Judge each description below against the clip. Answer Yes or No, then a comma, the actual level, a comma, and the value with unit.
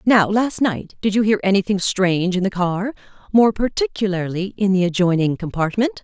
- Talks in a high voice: Yes, high, 200 Hz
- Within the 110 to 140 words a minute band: No, average, 170 wpm